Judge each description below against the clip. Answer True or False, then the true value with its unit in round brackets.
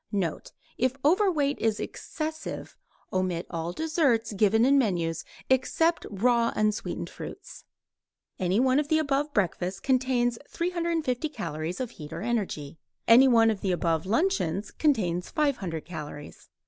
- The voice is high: True (230 Hz)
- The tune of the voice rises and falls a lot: True (7.6 semitones)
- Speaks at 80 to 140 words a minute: True (135 wpm)